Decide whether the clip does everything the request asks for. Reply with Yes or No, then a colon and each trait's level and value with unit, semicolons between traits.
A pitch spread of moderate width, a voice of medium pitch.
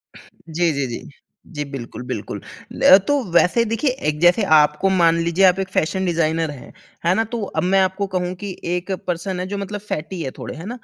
Yes: average, 3.1 semitones; medium, 180 Hz